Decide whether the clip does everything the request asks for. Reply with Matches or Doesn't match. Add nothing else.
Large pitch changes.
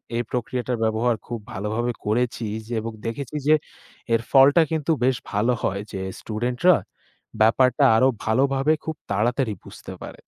Doesn't match